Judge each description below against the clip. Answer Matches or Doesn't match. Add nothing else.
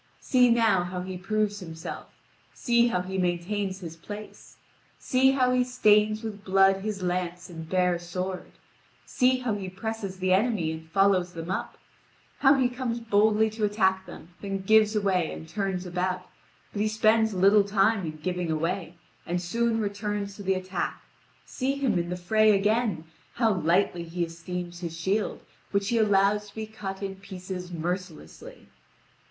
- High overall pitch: Matches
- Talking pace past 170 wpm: Doesn't match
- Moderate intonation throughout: Matches